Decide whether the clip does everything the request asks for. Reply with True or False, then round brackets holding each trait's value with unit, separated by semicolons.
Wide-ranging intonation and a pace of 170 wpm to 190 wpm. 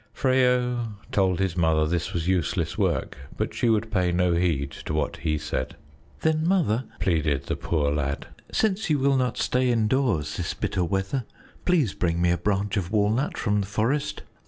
True (6.8 semitones; 180 wpm)